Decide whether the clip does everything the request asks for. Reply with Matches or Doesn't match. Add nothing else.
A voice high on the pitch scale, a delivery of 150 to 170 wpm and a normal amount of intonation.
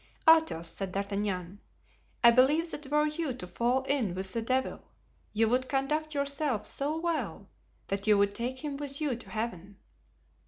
Doesn't match